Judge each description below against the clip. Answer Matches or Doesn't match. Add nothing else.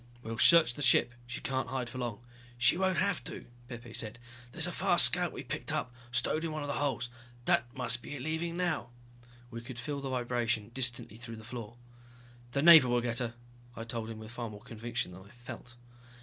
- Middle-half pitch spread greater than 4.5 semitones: Doesn't match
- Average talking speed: Doesn't match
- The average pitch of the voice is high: Doesn't match